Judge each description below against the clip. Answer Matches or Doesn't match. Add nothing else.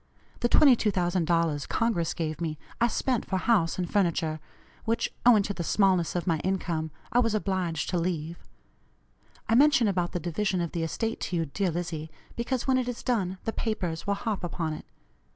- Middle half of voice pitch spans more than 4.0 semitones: Matches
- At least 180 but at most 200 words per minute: Matches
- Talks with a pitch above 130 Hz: Matches